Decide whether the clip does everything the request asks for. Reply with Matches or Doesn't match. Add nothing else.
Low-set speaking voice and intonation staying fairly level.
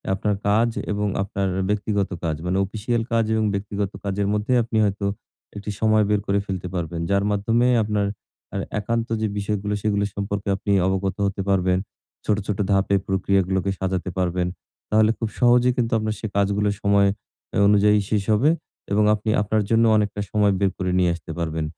Matches